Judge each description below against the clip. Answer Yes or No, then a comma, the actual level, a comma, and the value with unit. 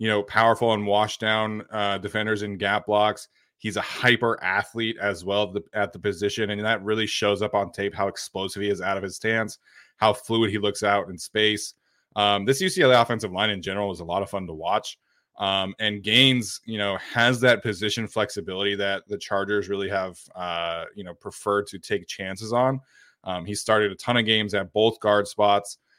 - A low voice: Yes, low, 105 Hz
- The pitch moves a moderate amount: No, narrow, 1.6 semitones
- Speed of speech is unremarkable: No, fast, 210 wpm